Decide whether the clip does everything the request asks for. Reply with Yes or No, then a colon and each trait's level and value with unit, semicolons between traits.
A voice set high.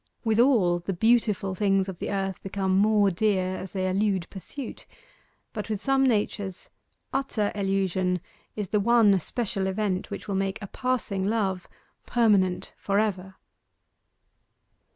Yes: high, 195 Hz